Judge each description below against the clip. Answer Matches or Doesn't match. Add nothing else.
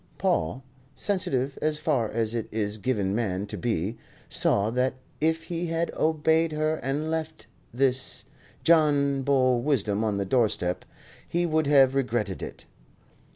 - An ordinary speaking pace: Matches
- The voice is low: Matches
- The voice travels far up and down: Matches